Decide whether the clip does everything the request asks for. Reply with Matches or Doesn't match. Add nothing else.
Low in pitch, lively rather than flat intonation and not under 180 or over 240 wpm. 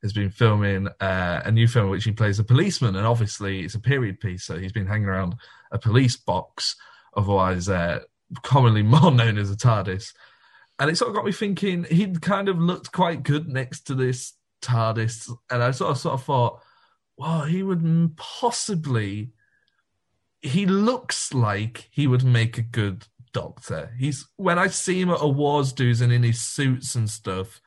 Matches